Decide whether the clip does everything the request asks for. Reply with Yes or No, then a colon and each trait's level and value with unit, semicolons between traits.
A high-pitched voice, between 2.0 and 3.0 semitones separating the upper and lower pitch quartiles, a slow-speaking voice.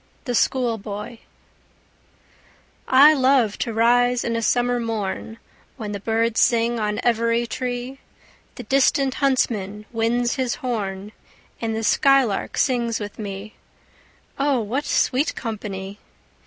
Yes: high, 230 Hz; average, 2.7 semitones; slow, 120 wpm